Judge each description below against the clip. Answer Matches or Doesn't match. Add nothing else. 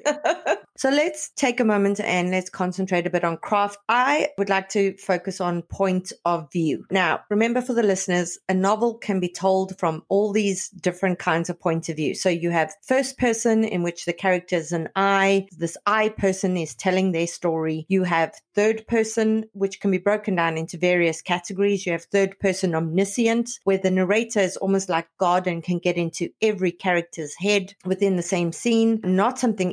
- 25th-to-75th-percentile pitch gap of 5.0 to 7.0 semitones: Doesn't match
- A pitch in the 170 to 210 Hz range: Matches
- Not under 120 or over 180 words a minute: Doesn't match